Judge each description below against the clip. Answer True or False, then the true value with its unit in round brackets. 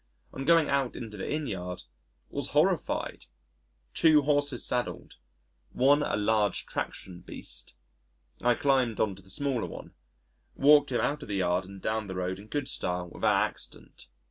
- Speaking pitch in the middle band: False (120 Hz)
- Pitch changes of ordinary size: False (6.7 semitones)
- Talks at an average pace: True (165 wpm)